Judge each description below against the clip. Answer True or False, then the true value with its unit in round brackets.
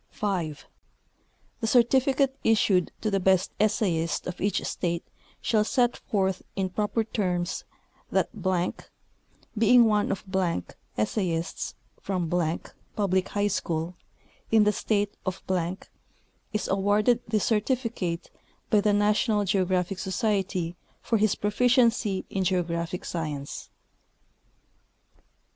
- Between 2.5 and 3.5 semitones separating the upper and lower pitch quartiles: True (3.2 semitones)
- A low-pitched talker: False (200 Hz)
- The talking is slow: True (105 wpm)